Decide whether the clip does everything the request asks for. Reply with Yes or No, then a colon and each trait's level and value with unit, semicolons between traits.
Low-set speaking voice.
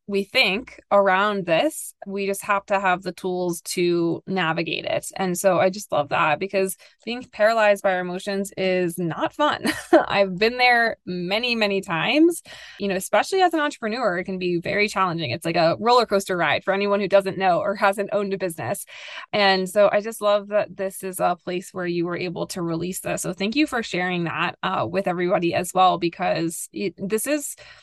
No: high, 195 Hz